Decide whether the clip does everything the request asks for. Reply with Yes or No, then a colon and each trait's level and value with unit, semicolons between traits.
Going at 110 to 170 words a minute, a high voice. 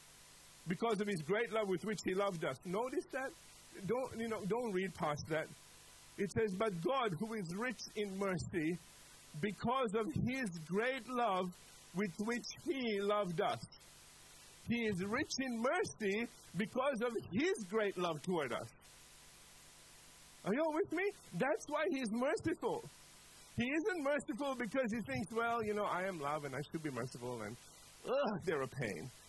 Yes: average, 165 wpm; high, 215 Hz